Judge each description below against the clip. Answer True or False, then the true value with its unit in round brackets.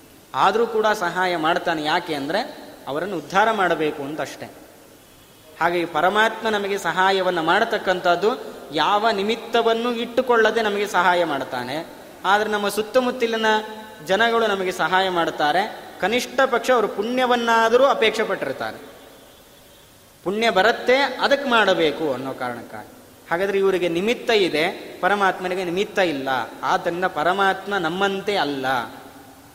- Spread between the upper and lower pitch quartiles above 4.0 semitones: True (4.5 semitones)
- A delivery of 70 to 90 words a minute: False (105 wpm)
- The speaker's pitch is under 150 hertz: False (195 Hz)